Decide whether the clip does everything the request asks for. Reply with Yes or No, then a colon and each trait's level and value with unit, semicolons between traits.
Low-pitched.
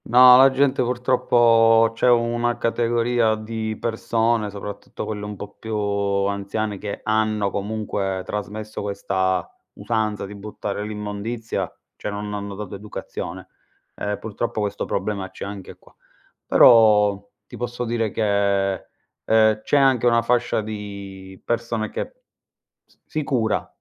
Yes: low, 110 Hz